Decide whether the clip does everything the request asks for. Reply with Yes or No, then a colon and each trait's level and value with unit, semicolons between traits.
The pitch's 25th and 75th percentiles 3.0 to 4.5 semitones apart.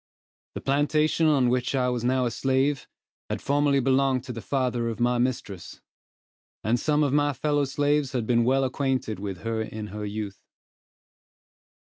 Yes: average, 3.3 semitones